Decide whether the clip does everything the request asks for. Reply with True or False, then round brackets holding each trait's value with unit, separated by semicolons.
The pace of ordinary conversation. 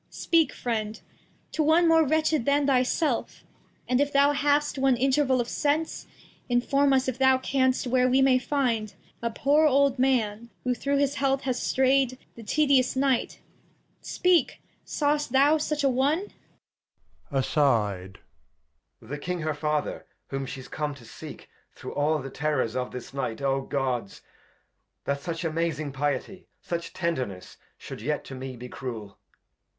True (155 wpm)